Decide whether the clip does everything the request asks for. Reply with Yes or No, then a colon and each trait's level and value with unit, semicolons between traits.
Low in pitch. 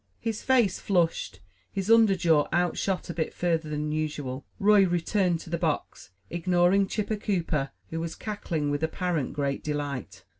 No: medium, 170 Hz